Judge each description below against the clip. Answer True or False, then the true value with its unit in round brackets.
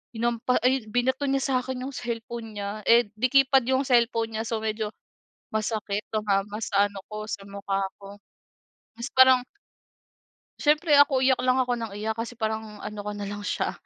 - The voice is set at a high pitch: True (230 Hz)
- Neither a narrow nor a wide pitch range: True (3.4 semitones)